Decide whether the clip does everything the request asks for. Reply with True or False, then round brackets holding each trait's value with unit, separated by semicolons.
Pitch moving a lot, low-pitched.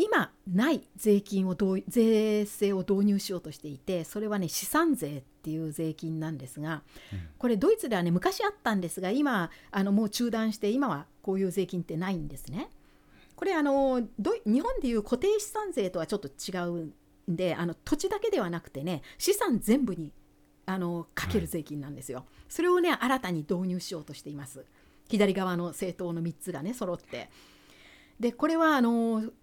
False (6.0 semitones; 195 Hz)